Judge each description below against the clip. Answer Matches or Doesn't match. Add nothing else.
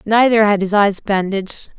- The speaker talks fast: Doesn't match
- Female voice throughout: Matches